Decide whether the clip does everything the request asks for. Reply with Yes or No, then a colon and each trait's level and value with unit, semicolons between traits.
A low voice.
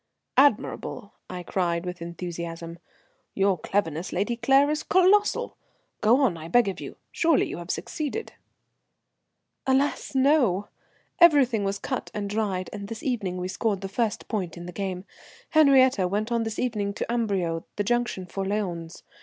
No: high, 205 Hz